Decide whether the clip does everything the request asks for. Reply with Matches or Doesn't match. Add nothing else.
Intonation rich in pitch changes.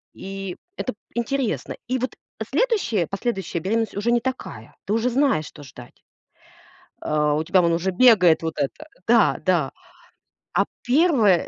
Matches